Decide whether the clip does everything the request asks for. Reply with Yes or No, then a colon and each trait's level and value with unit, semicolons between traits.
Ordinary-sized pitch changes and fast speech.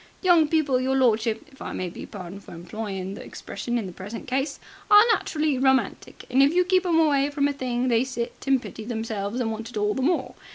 Yes: average, 4.6 semitones; fast, 230 wpm